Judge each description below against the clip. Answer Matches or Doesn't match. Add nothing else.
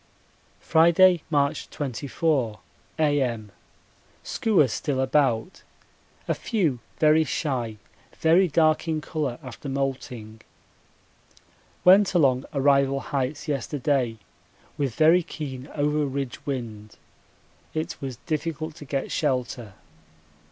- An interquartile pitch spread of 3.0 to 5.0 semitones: Matches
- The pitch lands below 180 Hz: Matches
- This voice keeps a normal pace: Doesn't match